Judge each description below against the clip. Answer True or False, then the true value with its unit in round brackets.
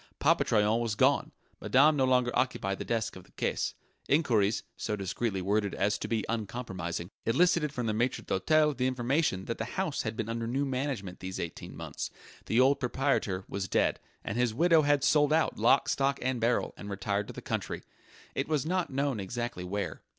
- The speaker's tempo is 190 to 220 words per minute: True (195 wpm)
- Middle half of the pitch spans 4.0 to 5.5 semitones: True (5.2 semitones)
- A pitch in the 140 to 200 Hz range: False (120 Hz)